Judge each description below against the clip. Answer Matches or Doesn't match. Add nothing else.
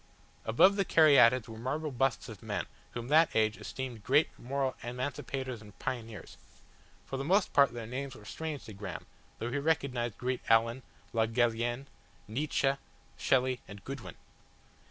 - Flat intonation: Doesn't match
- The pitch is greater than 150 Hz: Doesn't match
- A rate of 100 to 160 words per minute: Matches